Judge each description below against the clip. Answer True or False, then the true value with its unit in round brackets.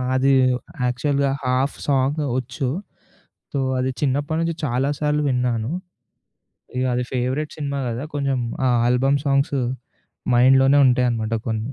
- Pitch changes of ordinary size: False (2.1 semitones)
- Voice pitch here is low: True (130 Hz)